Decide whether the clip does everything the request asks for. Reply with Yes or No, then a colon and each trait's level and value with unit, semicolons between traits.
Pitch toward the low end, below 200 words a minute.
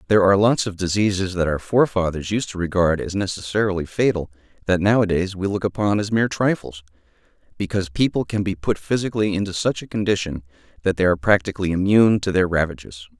Yes: very low, 95 Hz; average, 180 wpm